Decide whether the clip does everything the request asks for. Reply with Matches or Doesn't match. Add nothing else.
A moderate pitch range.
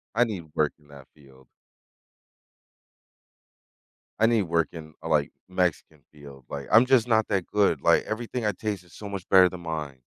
Doesn't match